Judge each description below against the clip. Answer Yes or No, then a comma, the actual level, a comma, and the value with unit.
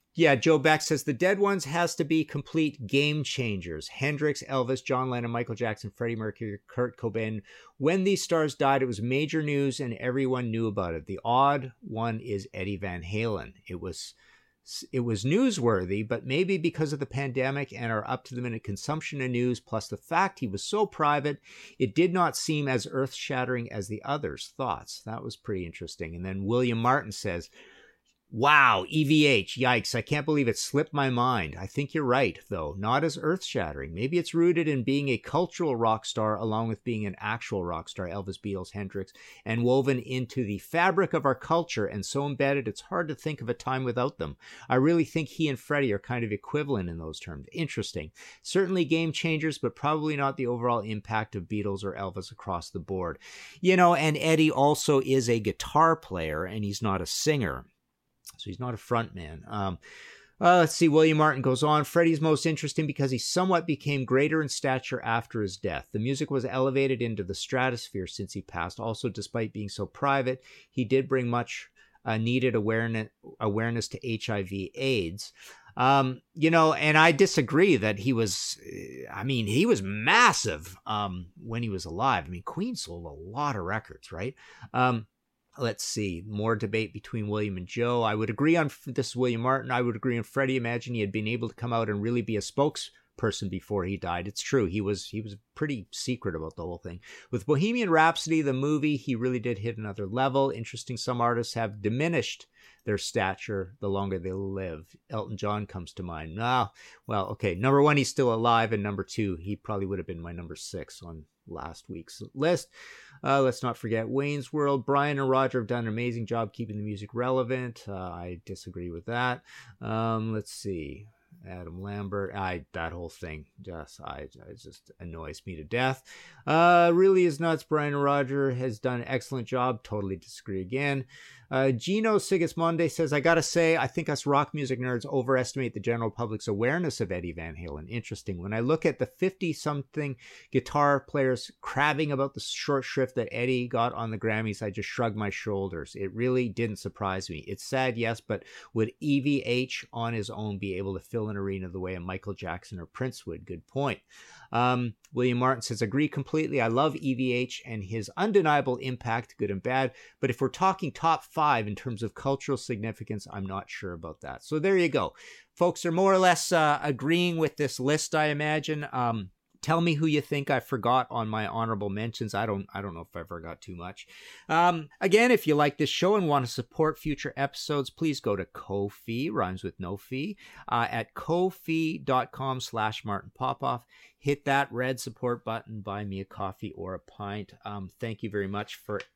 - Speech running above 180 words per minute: Yes, average, 195 wpm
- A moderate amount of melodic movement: No, wide, 5.7 semitones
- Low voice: Yes, low, 125 Hz